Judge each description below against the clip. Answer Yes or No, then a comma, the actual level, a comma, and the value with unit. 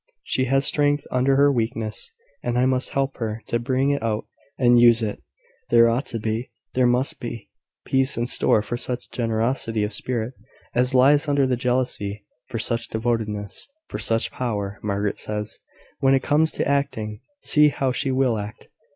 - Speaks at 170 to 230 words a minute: Yes, average, 175 wpm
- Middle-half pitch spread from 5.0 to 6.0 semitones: No, average, 3.0 semitones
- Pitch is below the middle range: Yes, low, 120 Hz